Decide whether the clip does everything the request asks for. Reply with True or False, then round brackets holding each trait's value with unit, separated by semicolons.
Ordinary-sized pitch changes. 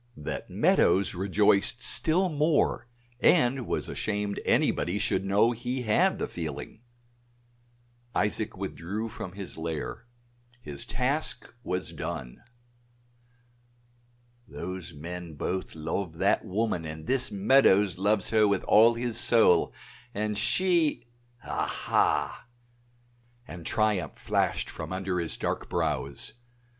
True (5.0 semitones)